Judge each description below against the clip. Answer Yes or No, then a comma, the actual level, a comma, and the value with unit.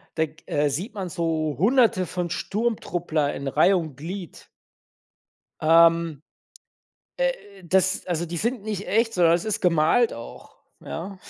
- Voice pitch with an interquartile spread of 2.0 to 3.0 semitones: No, average, 4.1 semitones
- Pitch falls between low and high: Yes, medium, 175 Hz